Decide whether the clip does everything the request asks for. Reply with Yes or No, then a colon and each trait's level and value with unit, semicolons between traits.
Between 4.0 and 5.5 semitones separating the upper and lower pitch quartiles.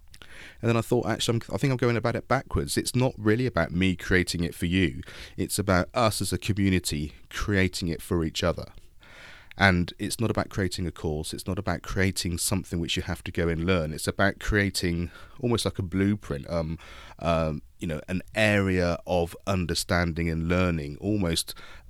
No: average, 3.1 semitones